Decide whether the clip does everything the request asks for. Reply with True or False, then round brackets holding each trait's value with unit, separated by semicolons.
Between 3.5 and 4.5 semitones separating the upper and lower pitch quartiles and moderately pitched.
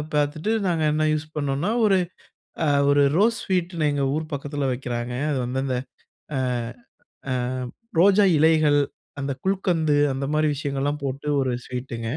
False (3.1 semitones; 145 Hz)